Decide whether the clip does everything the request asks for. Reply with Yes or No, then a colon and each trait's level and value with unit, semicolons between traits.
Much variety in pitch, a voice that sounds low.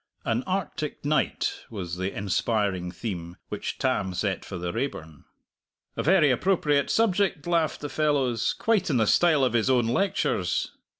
Yes: wide, 8.3 semitones; low, 125 Hz